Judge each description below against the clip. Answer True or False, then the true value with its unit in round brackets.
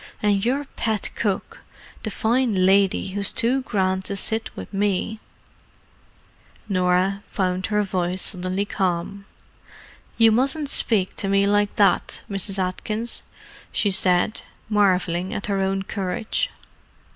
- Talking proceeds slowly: True (125 wpm)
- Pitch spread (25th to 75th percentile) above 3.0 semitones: False (2.5 semitones)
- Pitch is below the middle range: False (200 Hz)